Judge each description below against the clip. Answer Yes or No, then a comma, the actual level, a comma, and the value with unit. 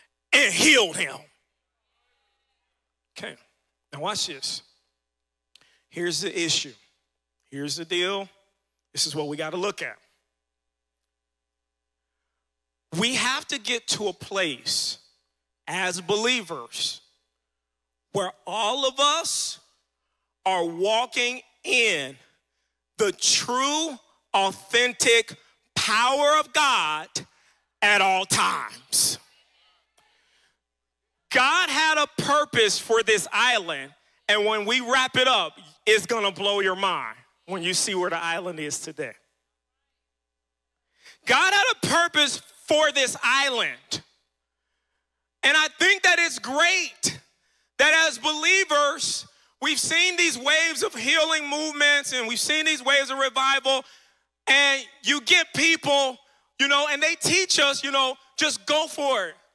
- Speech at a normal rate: No, slow, 120 wpm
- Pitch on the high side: Yes, high, 220 Hz